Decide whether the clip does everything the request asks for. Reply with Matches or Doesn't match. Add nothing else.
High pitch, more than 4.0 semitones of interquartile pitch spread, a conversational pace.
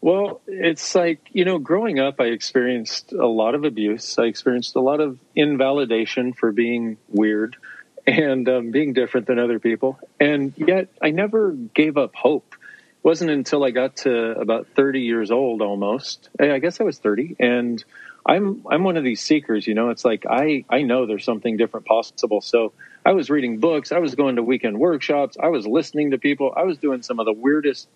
Doesn't match